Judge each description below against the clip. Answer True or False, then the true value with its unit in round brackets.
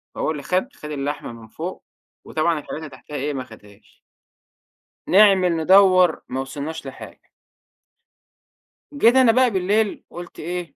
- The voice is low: False (165 Hz)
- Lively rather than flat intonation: False (5.0 semitones)